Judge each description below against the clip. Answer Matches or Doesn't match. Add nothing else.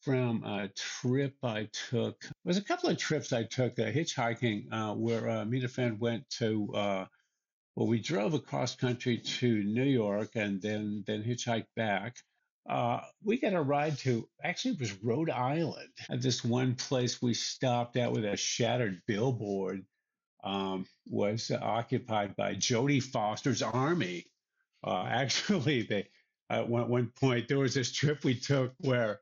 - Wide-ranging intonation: Doesn't match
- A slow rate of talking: Doesn't match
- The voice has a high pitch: Doesn't match